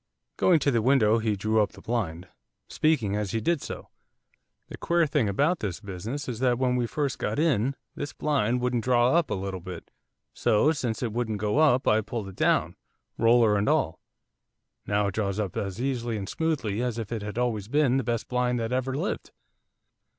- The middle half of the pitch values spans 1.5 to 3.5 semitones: No, average, 4.0 semitones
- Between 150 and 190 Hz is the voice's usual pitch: No, low, 115 Hz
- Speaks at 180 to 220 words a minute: Yes, average, 200 wpm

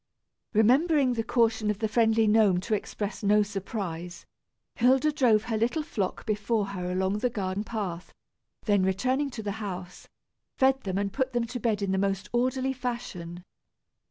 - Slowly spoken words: No, average, 165 wpm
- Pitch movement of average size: Yes, average, 3.8 semitones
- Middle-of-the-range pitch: No, high, 215 Hz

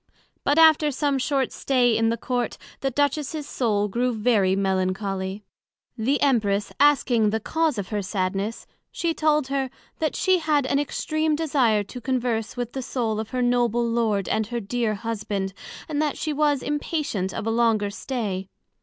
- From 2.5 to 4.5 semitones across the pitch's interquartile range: No, average, 5.2 semitones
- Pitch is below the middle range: No, high, 240 Hz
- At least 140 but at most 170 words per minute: Yes, average, 165 wpm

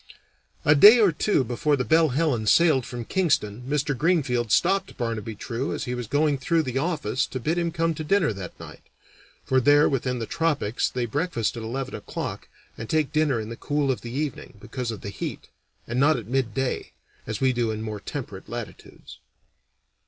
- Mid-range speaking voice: No, low, 130 Hz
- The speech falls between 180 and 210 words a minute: Yes, average, 195 wpm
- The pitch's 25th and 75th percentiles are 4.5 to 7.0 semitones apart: Yes, average, 4.8 semitones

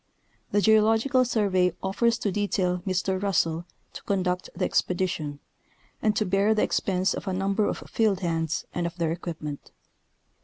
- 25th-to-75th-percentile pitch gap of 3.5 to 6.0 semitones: No, average, 2.8 semitones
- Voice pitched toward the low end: No, high, 190 Hz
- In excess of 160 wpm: No, average, 155 wpm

